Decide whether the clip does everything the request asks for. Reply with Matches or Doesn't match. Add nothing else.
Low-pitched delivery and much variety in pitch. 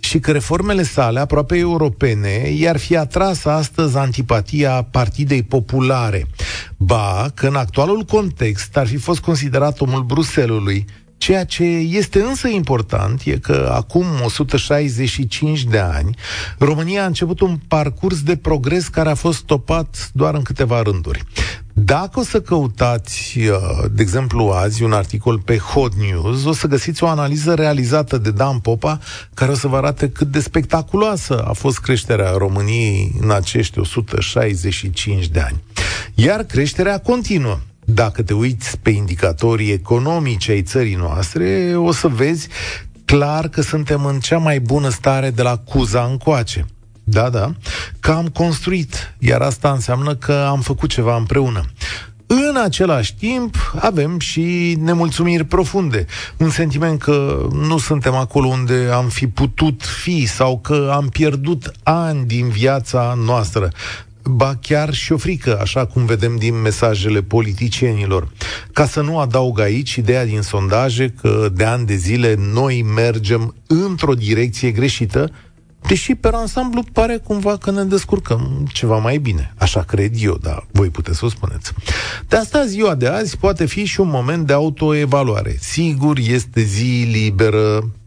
Matches